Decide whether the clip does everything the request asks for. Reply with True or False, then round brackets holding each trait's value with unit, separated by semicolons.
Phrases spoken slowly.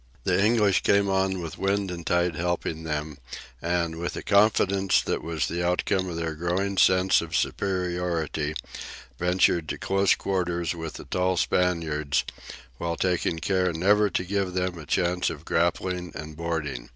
False (160 wpm)